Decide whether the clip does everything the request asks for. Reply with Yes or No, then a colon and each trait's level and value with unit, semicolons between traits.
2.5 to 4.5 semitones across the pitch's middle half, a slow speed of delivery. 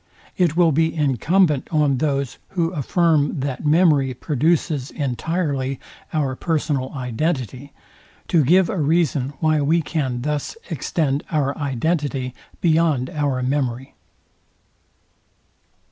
Yes: average, 3.5 semitones; slow, 110 wpm